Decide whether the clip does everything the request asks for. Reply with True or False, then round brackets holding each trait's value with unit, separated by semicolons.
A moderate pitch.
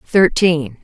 True (160 Hz)